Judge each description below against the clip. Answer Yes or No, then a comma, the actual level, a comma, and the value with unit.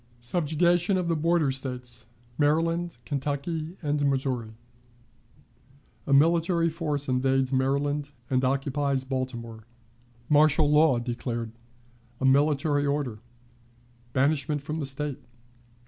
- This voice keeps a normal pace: No, slow, 100 wpm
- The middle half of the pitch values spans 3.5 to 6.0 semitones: No, average, 2.8 semitones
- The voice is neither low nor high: Yes, medium, 145 Hz